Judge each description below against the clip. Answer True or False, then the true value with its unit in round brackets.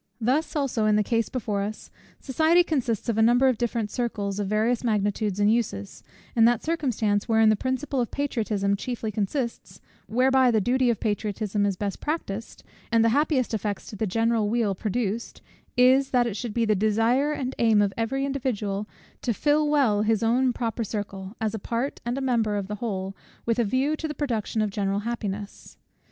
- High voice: True (225 Hz)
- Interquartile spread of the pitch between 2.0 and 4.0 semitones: True (3.5 semitones)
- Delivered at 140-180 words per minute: False (190 wpm)